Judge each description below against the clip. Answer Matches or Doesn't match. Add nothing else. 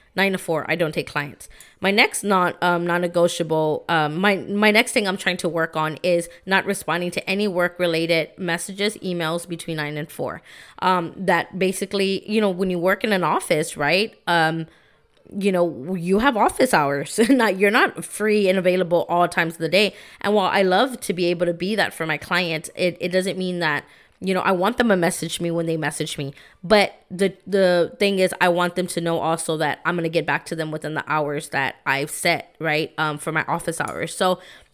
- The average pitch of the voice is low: Doesn't match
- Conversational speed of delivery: Doesn't match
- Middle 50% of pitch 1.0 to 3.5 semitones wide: Matches